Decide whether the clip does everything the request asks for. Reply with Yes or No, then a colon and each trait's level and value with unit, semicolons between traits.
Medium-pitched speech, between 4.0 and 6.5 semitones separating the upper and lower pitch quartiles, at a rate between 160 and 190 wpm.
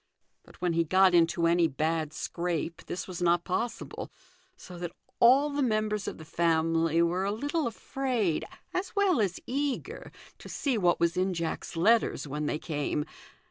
Yes: medium, 175 Hz; wide, 5.6 semitones; average, 170 wpm